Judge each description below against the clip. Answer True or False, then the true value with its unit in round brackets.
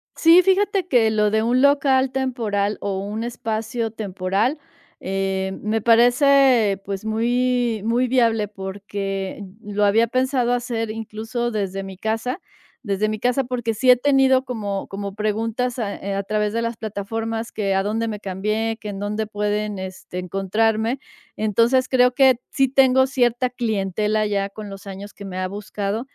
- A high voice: True (220 Hz)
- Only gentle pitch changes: False (3.4 semitones)